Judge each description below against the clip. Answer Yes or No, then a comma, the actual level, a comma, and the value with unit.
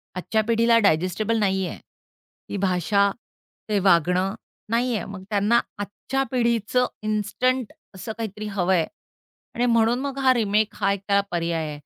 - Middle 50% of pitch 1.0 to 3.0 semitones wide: No, average, 3.5 semitones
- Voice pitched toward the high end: Yes, high, 210 Hz